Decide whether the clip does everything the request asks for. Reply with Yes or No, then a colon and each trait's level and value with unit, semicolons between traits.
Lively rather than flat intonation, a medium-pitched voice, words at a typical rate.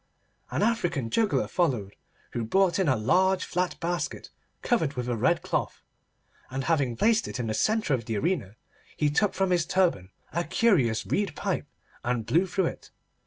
Yes: wide, 7.7 semitones; medium, 165 Hz; average, 175 wpm